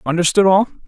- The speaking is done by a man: No, female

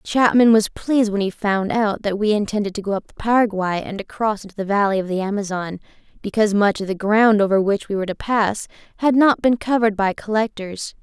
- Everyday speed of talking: No, fast, 220 wpm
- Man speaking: No, female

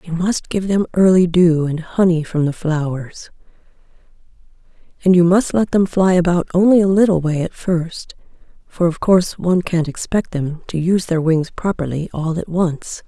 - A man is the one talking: No, female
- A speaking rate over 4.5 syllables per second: Yes, 4.9 syllables/s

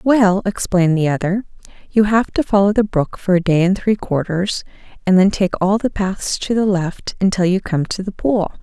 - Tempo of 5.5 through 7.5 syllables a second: No, 5.0 syllables/s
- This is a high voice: Yes, high, 195 Hz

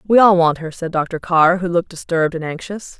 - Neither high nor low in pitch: Yes, medium, 170 Hz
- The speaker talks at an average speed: No, fast, 240 wpm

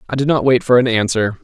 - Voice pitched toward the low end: Yes, low, 120 Hz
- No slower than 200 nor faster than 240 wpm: No, fast, 290 wpm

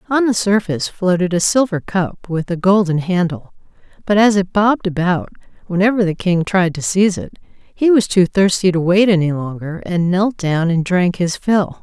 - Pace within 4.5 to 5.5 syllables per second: Yes, 4.9 syllables/s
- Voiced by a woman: Yes, female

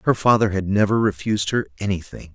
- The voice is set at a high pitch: No, low, 100 Hz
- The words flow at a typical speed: Yes, average, 180 wpm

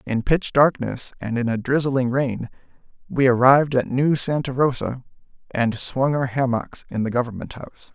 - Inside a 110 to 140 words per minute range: No, average, 165 wpm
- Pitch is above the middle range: No, low, 130 Hz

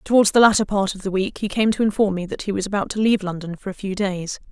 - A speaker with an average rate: No, fast, 305 wpm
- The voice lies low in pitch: No, high, 200 Hz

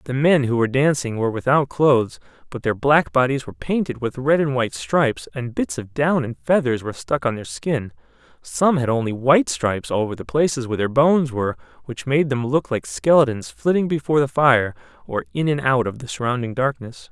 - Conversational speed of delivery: No, fast, 210 wpm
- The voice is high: No, low, 130 Hz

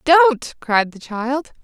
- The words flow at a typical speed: Yes, average, 145 wpm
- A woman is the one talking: Yes, female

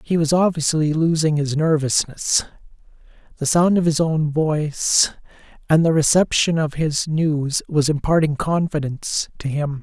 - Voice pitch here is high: No, medium, 155 Hz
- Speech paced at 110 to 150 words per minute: Yes, average, 140 wpm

